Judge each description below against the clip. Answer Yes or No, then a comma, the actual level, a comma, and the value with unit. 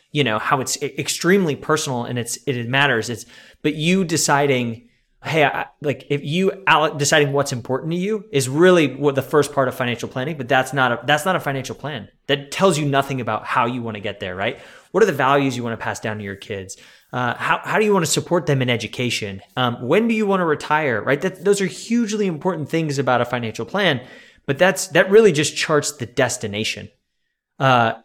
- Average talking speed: No, fast, 220 wpm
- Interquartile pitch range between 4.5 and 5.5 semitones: Yes, average, 5.2 semitones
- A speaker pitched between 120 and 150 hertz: Yes, medium, 140 Hz